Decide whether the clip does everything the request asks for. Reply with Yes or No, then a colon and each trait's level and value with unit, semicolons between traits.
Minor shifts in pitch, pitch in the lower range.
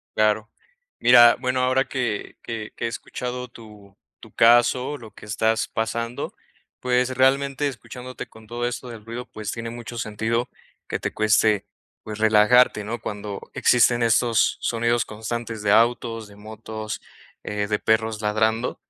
Yes: narrow, 2.2 semitones; low, 115 Hz